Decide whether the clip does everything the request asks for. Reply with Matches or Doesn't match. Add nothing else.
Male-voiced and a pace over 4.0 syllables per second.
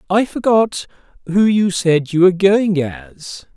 Doesn't match